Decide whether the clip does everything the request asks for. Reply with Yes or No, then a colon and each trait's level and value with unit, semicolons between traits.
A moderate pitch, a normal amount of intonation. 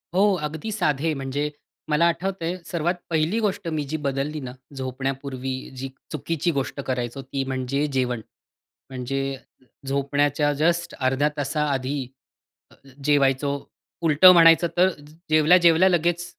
Yes: medium, 145 Hz; average, 3.7 semitones